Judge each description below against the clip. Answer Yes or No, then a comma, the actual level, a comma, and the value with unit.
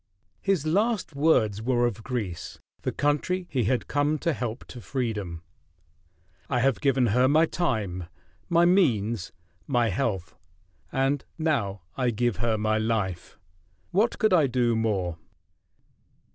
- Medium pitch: No, low, 125 Hz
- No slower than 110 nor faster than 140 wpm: Yes, slow, 135 wpm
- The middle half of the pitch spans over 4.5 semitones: Yes, wide, 5.4 semitones